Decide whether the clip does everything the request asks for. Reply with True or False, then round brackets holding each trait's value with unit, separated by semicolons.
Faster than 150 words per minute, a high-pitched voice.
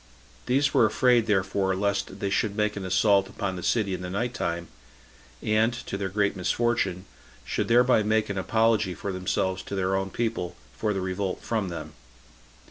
False (180 wpm; 100 Hz)